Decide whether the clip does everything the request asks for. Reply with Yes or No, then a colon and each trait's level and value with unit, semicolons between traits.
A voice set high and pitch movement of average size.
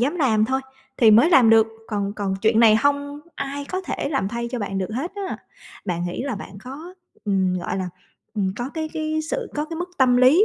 No: high, 245 Hz; wide, 6.4 semitones